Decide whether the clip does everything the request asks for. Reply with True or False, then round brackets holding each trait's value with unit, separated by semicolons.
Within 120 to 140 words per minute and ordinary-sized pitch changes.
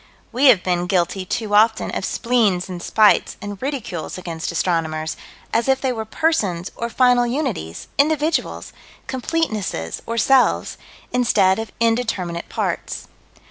False (135 wpm; 5.7 semitones)